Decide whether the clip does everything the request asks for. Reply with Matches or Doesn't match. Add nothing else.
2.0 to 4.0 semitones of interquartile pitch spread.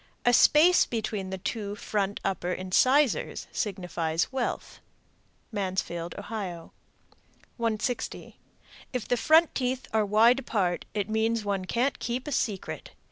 Doesn't match